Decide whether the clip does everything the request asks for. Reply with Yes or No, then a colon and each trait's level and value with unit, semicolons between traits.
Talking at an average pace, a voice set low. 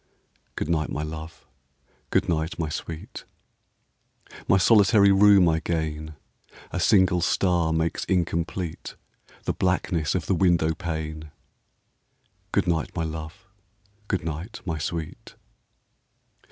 No: slow, 115 wpm; very low, 85 Hz